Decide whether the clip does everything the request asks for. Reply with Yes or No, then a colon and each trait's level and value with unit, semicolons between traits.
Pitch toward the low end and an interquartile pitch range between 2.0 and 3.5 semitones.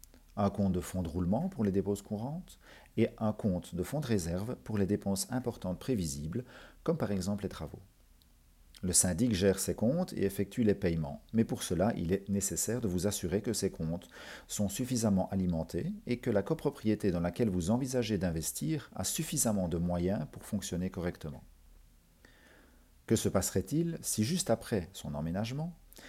No: low, 100 Hz; average, 4.6 semitones